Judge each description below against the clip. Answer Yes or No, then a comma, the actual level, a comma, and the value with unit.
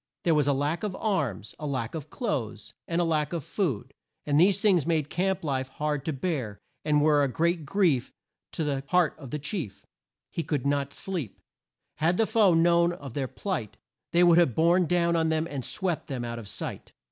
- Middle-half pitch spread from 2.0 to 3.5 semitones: No, average, 4.0 semitones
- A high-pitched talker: No, medium, 155 Hz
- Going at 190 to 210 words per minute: Yes, fast, 205 wpm